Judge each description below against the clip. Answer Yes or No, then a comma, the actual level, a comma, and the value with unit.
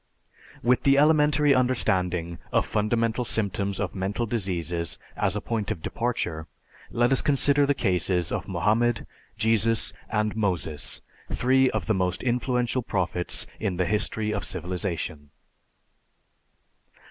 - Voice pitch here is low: Yes, low, 110 Hz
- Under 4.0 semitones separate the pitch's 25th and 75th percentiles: No, average, 5.2 semitones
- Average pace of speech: No, slow, 125 wpm